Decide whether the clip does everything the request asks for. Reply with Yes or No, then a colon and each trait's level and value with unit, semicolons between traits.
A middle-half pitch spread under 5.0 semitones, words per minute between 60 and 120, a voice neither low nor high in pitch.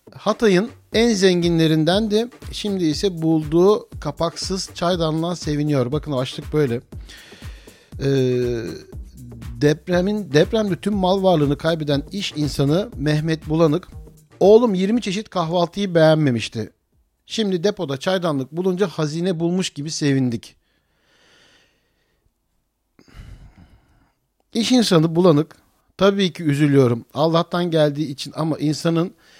Yes: average, 4.3 semitones; average, 100 wpm; medium, 165 Hz